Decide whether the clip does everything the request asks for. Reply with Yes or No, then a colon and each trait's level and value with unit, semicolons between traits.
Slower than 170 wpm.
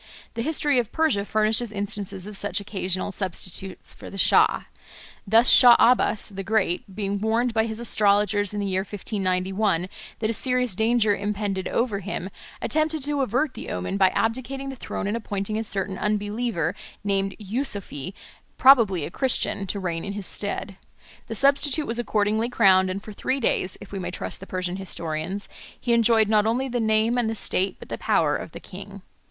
No: average, 180 wpm